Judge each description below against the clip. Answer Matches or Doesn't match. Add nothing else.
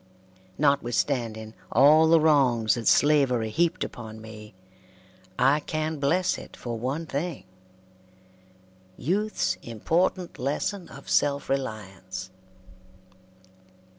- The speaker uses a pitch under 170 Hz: Matches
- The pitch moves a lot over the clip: Matches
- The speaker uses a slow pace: Matches